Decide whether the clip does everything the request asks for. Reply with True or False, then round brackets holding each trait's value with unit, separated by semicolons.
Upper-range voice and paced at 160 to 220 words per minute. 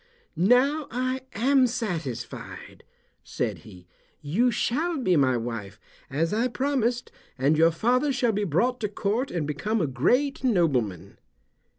False (210 Hz; 135 wpm)